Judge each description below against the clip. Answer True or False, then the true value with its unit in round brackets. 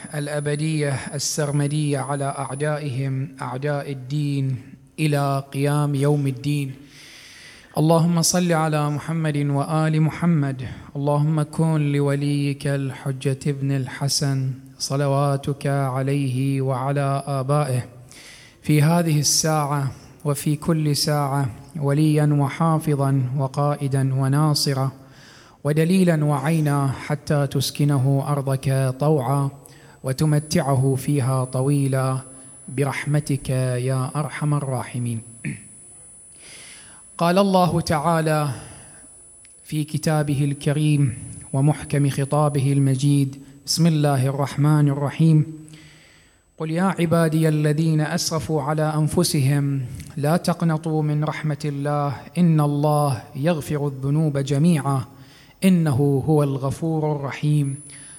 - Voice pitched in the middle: True (145 Hz)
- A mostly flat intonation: True (1.8 semitones)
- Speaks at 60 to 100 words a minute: True (85 wpm)